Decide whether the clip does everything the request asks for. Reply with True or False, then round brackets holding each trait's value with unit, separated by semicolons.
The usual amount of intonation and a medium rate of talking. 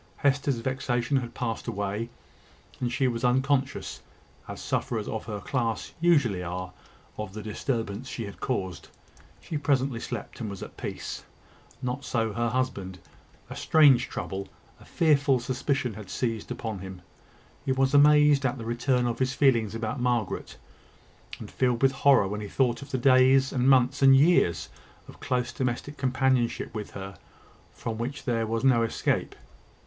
True (3.2 semitones; 160 wpm)